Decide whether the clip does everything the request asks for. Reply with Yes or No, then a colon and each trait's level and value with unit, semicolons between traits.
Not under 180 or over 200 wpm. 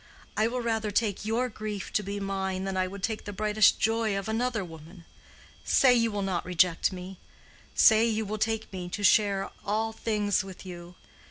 Yes: average, 185 wpm